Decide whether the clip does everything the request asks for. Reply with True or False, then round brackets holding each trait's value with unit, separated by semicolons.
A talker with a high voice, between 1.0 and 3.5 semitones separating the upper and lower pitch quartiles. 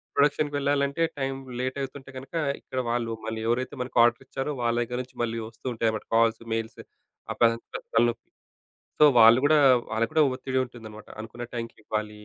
False (120 Hz; 2.7 semitones)